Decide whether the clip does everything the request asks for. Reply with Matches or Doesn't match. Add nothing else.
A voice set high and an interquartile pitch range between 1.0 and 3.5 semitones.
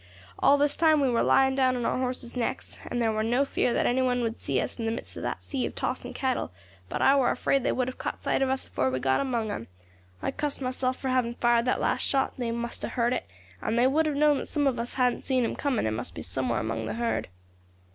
Matches